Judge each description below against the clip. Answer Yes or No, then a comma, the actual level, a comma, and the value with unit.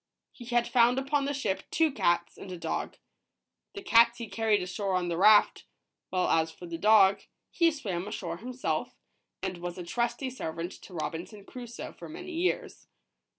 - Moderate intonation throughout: No, wide, 6.1 semitones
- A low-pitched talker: No, high, 215 Hz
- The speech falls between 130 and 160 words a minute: No, average, 175 wpm